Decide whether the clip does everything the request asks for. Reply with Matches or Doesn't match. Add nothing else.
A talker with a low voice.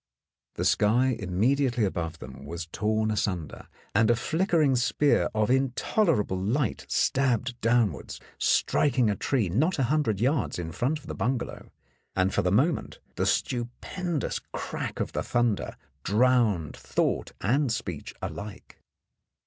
Matches